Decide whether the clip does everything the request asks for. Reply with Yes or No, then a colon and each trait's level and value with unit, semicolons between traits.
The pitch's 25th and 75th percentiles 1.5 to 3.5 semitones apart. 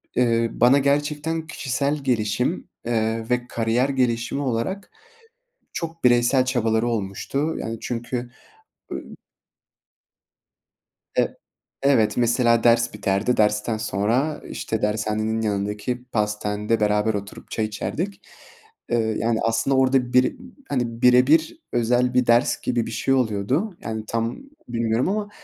Yes: average, 2.8 semitones